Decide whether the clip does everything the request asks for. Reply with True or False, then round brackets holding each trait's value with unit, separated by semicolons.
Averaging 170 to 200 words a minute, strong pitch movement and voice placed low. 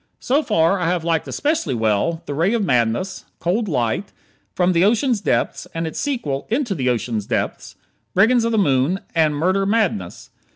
False (175 wpm; 7.3 semitones; 175 Hz)